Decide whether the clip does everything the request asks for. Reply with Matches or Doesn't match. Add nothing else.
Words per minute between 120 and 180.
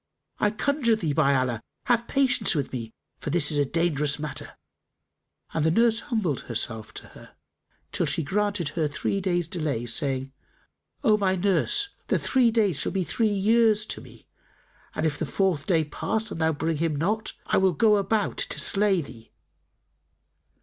Matches